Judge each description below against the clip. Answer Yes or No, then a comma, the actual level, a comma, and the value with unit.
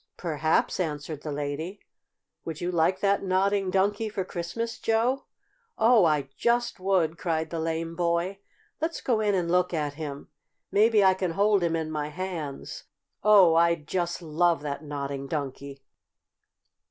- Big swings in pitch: No, average, 4.1 semitones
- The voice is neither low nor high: Yes, medium, 170 Hz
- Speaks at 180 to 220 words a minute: No, average, 155 wpm